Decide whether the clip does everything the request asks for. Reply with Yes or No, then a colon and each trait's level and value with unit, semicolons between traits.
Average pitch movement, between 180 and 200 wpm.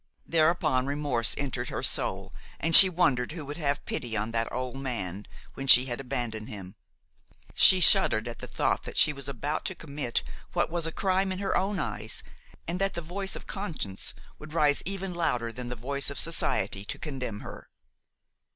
No: wide, 5.8 semitones; average, 190 wpm